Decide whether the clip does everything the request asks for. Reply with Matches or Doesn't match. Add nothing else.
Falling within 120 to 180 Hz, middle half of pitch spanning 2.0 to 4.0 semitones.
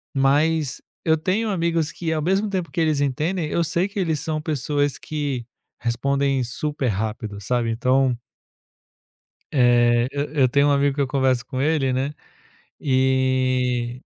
Matches